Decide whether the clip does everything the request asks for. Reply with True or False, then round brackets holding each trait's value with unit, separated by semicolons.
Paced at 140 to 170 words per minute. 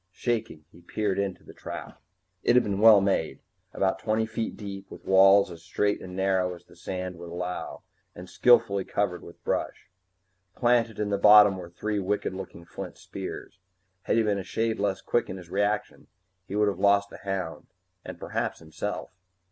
False (185 wpm)